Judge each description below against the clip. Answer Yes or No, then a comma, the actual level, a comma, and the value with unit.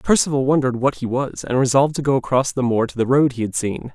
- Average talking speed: No, fast, 275 wpm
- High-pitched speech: No, low, 130 Hz